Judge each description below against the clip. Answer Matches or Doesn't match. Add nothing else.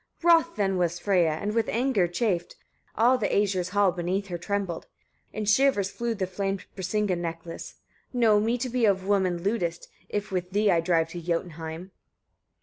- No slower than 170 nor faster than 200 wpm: Matches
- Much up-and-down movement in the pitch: Doesn't match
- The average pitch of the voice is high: Matches